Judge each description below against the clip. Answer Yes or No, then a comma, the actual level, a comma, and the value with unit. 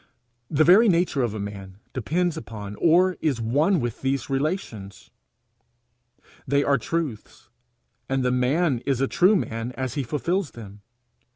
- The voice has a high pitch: No, low, 135 Hz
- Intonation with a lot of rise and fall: Yes, wide, 6.3 semitones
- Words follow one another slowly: No, average, 150 wpm